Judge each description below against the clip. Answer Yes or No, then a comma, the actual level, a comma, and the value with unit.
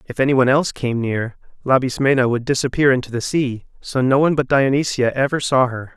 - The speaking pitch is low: Yes, low, 130 Hz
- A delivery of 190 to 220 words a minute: Yes, average, 200 wpm